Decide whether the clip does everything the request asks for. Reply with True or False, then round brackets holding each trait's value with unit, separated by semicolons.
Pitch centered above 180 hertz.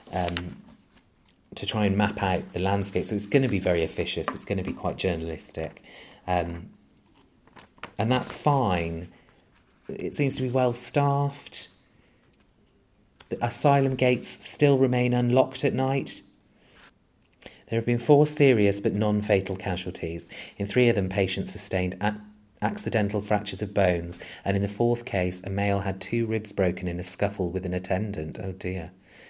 False (100 Hz)